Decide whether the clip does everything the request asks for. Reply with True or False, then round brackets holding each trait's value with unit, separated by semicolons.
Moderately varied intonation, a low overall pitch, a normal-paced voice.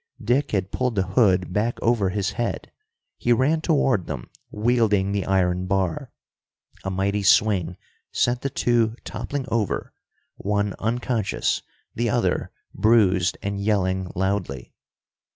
False (3.8 semitones; 100 Hz; 130 wpm)